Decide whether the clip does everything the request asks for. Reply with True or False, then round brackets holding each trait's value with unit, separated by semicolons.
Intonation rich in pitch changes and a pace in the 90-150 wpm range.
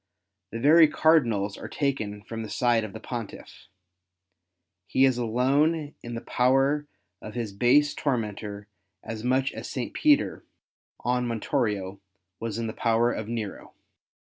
False (3.7 semitones; 140 wpm)